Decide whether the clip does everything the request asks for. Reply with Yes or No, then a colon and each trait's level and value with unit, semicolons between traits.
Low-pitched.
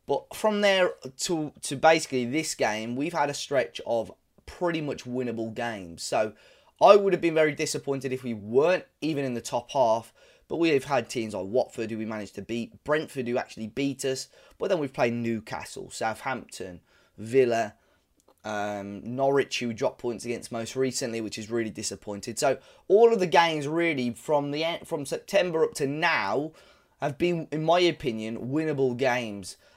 Yes: low, 130 Hz